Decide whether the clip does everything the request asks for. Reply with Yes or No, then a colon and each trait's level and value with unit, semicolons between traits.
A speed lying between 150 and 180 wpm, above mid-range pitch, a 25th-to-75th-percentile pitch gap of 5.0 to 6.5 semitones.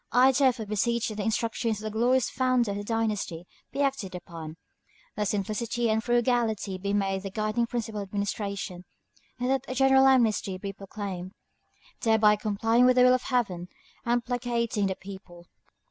No: average, 170 wpm; high, 220 Hz; average, 3.5 semitones